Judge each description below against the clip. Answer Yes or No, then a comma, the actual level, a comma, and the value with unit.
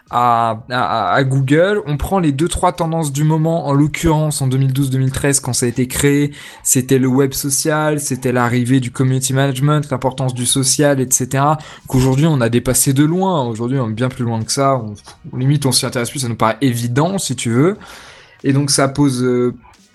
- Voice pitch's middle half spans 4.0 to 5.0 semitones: No, average, 2.8 semitones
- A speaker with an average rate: Yes, average, 200 wpm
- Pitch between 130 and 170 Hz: Yes, low, 135 Hz